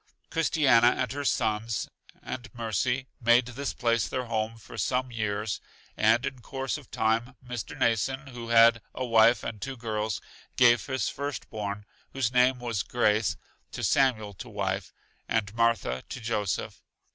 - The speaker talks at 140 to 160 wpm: Yes, average, 155 wpm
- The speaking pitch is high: No, low, 115 Hz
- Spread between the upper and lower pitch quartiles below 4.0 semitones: Yes, narrow, 2.6 semitones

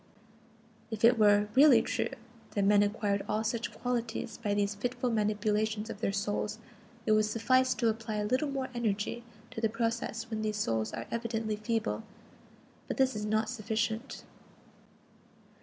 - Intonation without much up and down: Yes, narrow, 1.9 semitones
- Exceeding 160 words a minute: No, average, 155 wpm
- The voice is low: No, high, 220 Hz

